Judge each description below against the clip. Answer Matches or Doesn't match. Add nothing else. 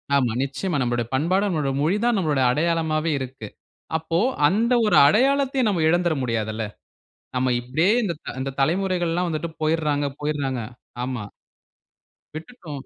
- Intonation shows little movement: Doesn't match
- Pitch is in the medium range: Matches